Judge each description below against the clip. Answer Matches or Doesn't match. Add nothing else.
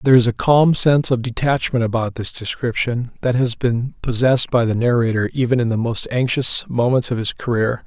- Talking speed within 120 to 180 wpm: Doesn't match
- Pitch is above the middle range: Doesn't match